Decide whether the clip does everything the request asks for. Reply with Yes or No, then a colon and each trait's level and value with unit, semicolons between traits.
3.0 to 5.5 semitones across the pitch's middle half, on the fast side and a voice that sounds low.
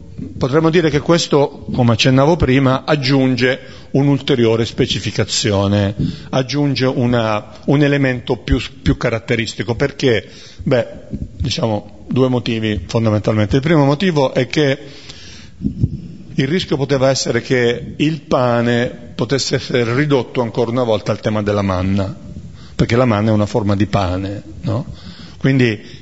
No: average, 4.2 semitones; average, 125 wpm; low, 125 Hz